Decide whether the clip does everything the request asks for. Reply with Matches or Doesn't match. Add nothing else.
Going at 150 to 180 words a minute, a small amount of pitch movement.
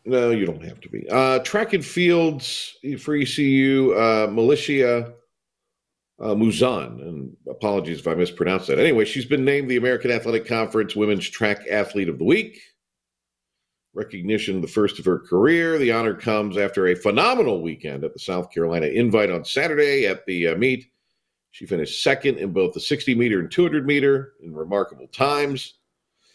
Doesn't match